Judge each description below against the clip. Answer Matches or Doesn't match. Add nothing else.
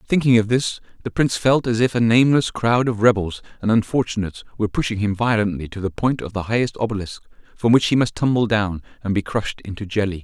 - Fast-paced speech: Matches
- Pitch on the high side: Doesn't match